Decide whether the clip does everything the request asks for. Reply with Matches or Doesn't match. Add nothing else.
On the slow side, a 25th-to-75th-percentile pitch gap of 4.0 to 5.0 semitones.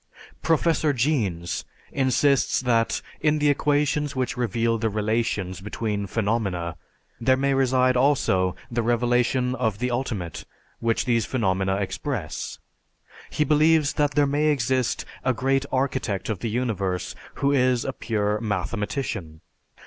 Matches